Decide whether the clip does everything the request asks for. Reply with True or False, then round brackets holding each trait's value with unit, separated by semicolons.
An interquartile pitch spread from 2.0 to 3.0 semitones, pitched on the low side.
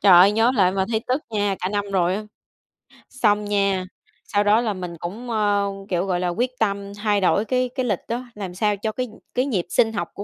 False (2.7 semitones; 205 Hz)